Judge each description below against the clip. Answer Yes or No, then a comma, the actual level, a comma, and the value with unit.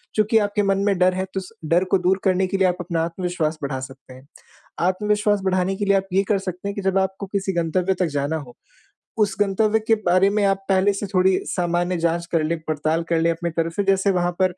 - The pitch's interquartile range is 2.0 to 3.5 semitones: Yes, narrow, 2.6 semitones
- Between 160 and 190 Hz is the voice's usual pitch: Yes, medium, 185 Hz